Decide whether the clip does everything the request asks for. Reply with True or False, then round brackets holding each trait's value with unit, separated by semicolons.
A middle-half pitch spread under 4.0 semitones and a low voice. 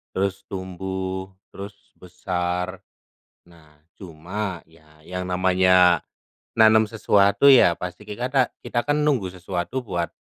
True (2.8 semitones; 95 Hz)